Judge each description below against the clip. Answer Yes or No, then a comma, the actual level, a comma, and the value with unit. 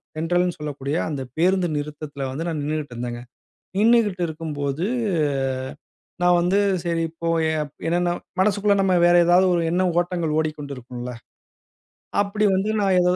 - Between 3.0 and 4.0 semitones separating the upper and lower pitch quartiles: Yes, average, 3.6 semitones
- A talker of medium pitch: Yes, medium, 165 Hz